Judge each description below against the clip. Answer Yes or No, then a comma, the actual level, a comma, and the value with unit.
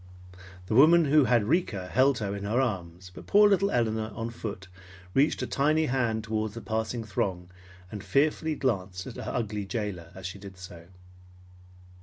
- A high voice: No, low, 110 Hz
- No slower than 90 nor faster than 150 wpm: No, average, 175 wpm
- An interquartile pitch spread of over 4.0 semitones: Yes, wide, 5.5 semitones